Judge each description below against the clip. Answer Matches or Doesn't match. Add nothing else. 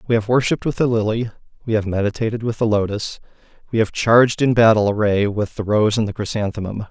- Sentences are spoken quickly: Matches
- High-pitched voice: Doesn't match